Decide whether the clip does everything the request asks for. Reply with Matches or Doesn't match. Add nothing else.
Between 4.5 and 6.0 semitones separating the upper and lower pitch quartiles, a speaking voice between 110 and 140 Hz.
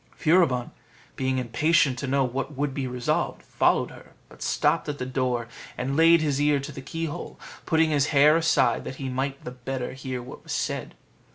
Doesn't match